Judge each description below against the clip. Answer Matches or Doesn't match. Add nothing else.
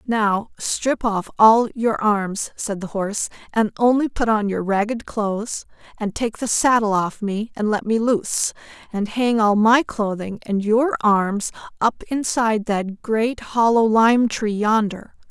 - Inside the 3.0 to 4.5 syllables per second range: Matches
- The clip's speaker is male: Doesn't match